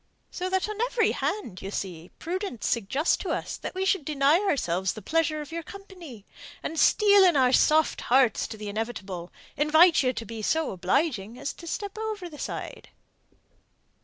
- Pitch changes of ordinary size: No, wide, 8.8 semitones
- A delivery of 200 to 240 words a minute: No, average, 175 wpm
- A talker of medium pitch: No, very high, 300 Hz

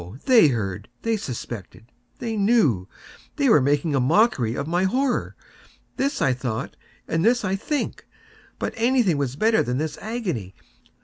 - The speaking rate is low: Yes, slow, 130 wpm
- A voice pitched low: No, medium, 165 Hz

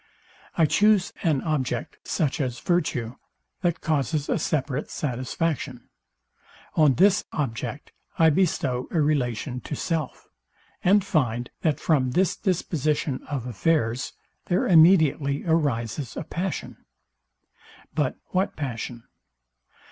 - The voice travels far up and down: No, average, 4.5 semitones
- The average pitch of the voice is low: No, medium, 150 Hz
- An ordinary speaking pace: No, slow, 110 wpm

